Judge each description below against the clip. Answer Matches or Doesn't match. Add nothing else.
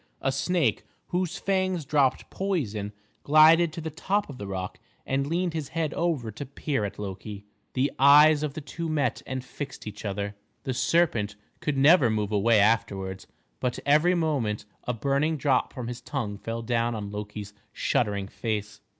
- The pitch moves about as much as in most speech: Doesn't match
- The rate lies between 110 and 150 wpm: Doesn't match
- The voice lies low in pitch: Matches